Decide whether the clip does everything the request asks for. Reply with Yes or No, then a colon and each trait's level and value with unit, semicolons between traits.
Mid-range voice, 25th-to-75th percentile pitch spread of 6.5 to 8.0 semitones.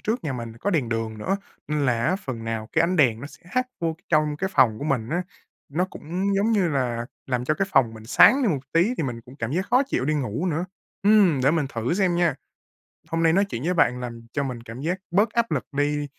Yes: medium, 150 Hz; wide, 6.8 semitones